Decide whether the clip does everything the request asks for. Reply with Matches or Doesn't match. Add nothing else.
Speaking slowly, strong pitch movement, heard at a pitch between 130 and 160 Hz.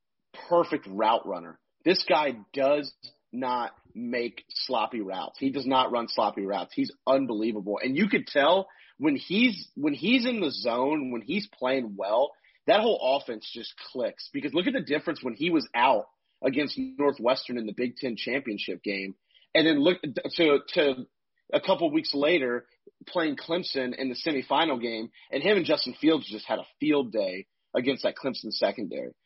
Doesn't match